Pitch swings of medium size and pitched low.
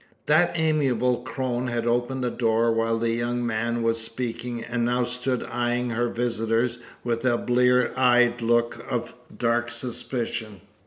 No: narrow, 1.1 semitones; low, 120 Hz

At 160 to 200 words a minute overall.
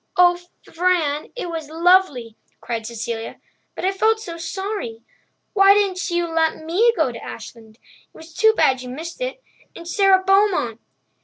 No: average, 150 wpm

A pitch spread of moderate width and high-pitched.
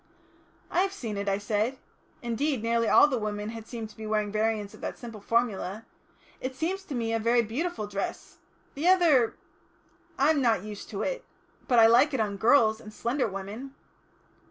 Yes: average, 3.9 semitones; high, 230 Hz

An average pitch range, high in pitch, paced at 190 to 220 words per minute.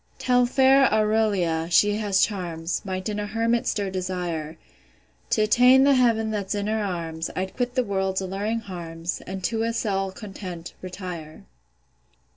No: average, 3.7 semitones; high, 200 Hz; average, 155 wpm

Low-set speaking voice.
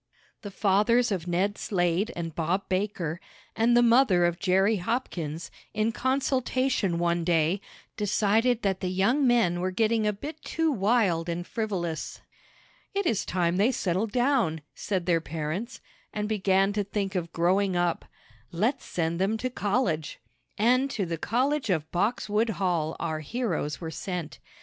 No: high, 195 Hz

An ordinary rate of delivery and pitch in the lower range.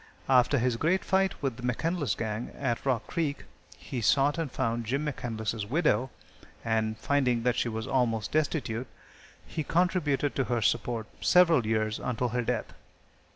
Yes: average, 160 wpm; low, 125 Hz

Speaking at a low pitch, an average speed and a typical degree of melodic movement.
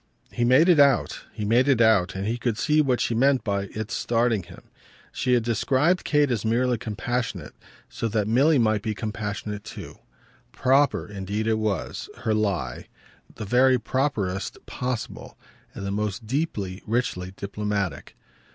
Yes: low, 110 Hz; average, 160 wpm; average, 3.6 semitones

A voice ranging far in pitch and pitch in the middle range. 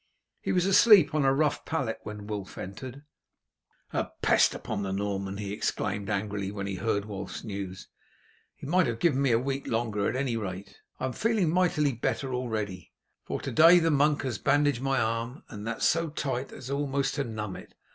No: wide, 5.8 semitones; low, 120 Hz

